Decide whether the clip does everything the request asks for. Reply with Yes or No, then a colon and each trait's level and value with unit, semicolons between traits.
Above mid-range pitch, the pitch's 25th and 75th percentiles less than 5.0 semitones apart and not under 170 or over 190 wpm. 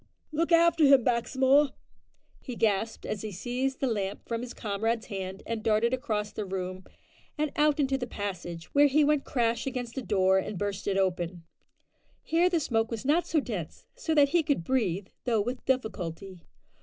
No: high, 230 Hz; wide, 5.6 semitones; average, 180 wpm